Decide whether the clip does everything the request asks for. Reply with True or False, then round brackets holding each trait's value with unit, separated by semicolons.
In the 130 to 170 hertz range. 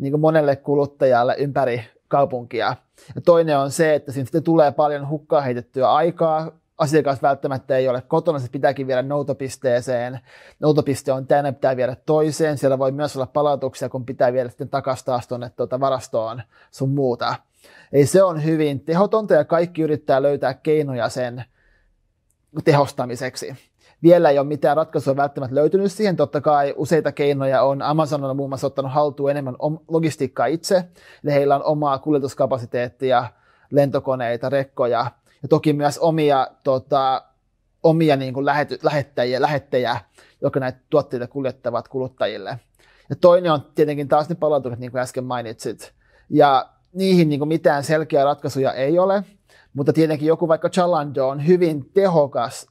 True (140 Hz)